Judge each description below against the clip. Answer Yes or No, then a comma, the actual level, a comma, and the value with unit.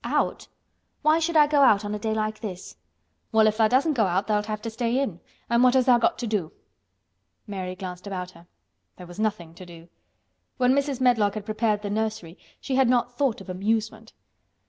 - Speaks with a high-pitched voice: Yes, high, 215 Hz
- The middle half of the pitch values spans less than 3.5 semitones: No, average, 4.0 semitones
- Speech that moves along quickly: Yes, fast, 210 wpm